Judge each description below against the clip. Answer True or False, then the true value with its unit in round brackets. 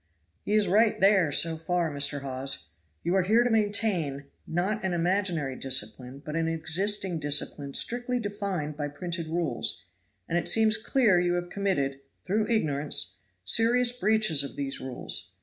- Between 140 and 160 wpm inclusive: True (155 wpm)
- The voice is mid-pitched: True (175 Hz)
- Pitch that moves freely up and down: True (6.2 semitones)